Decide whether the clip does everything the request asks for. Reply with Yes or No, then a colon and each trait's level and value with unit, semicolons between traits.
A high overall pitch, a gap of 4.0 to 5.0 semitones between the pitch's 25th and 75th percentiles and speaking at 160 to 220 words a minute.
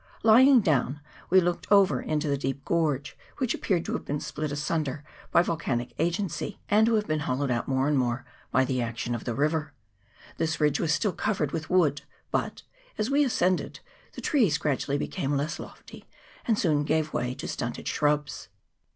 No: medium, 150 Hz; average, 4.7 semitones; average, 185 wpm